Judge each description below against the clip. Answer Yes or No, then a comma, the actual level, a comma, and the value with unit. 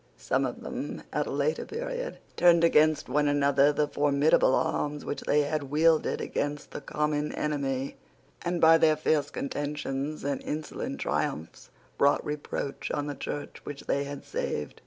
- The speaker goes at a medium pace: Yes, average, 155 wpm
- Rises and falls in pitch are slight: Yes, narrow, 1.5 semitones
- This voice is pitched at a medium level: Yes, medium, 145 Hz